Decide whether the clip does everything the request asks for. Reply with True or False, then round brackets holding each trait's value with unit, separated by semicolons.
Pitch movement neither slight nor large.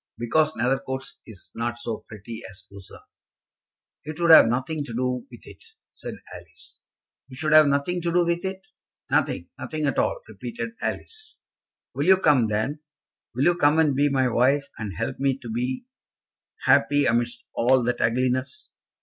True (4.6 semitones)